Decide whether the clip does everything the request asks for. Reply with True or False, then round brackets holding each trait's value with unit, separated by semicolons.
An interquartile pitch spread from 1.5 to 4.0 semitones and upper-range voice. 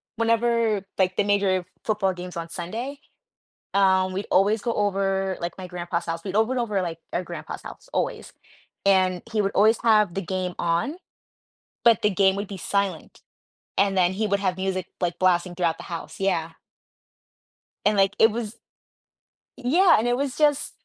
True (2.9 semitones; 195 Hz)